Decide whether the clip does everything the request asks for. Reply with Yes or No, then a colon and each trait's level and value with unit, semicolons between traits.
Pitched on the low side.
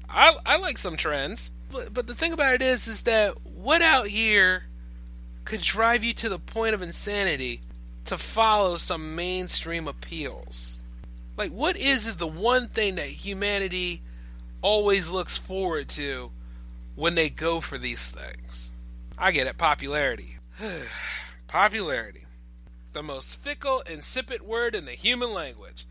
No: medium, 175 Hz